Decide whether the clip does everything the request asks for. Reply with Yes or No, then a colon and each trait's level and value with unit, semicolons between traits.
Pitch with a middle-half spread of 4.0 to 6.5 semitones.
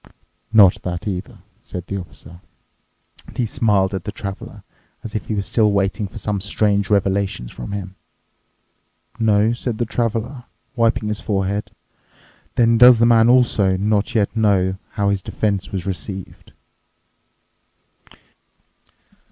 No: narrow, 2.6 semitones